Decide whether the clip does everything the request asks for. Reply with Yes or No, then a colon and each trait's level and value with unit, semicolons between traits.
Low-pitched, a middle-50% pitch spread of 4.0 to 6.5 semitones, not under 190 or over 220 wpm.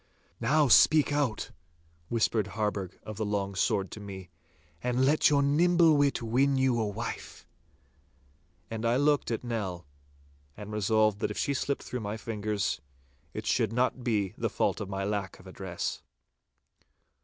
No: low, 110 Hz; average, 4.5 semitones; average, 155 wpm